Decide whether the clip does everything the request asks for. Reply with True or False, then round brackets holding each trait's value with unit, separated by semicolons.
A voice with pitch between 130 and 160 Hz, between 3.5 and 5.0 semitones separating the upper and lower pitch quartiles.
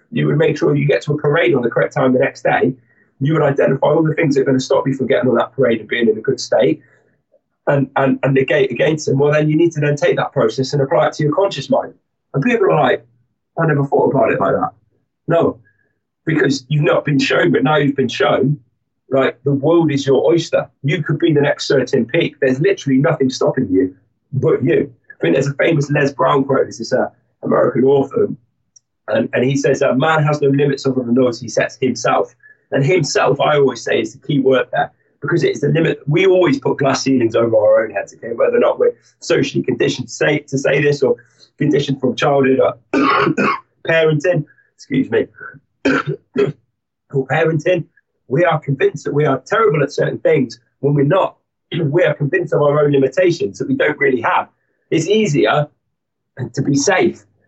False (140 Hz; 2.9 semitones)